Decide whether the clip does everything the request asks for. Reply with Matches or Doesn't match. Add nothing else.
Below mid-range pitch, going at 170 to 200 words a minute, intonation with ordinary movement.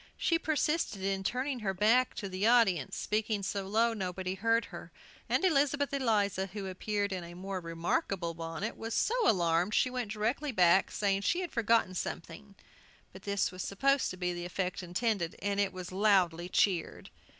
Doesn't match